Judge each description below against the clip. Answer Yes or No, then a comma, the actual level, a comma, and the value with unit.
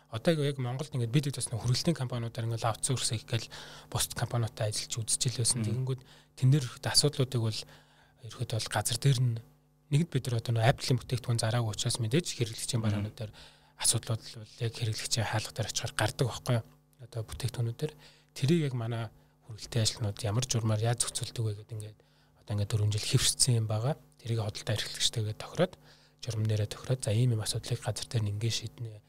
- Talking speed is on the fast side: Yes, fast, 165 wpm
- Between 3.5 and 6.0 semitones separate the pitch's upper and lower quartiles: No, average, 2.8 semitones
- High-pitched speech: No, low, 120 Hz